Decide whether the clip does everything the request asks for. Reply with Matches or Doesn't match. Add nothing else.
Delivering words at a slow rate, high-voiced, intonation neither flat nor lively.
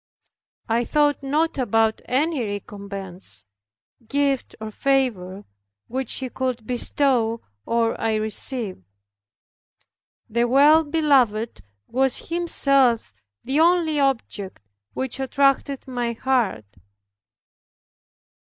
Matches